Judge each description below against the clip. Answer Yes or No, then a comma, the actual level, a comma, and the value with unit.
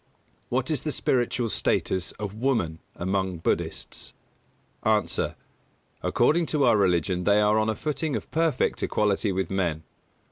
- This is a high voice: No, low, 105 Hz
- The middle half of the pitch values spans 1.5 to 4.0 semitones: No, wide, 5.6 semitones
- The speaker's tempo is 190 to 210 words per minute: No, average, 140 wpm